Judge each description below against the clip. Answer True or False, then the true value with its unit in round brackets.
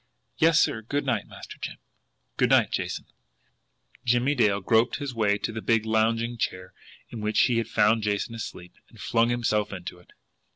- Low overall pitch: True (115 Hz)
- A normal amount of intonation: False (2.3 semitones)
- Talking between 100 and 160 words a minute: False (175 wpm)